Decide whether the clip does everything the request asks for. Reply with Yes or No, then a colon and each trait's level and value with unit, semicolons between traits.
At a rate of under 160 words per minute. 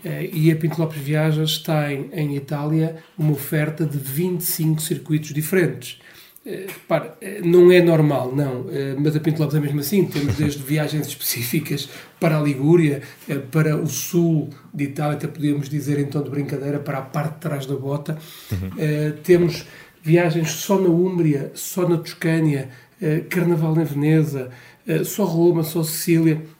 No: average, 165 wpm